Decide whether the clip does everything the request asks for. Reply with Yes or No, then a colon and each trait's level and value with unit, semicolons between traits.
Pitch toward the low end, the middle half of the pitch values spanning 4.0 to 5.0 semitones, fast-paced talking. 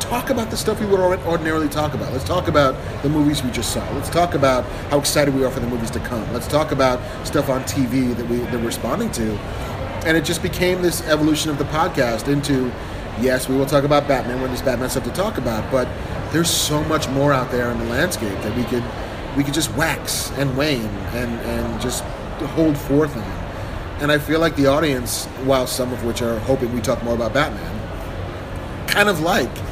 Yes: low, 130 Hz; average, 4.3 semitones; fast, 220 wpm